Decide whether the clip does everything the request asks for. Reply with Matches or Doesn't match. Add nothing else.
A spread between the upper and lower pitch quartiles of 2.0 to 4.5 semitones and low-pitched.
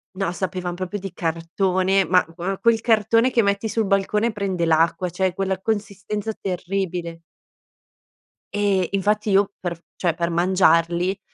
Doesn't match